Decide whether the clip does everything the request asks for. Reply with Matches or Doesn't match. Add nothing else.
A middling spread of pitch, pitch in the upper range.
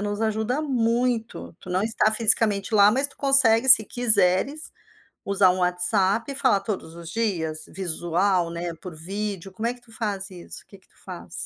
Matches